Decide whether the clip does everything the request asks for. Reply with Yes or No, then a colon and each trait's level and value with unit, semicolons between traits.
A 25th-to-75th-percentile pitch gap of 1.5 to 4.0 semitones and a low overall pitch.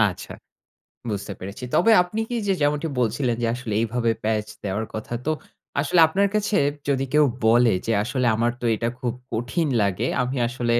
No: average, 4.7 semitones; low, 120 Hz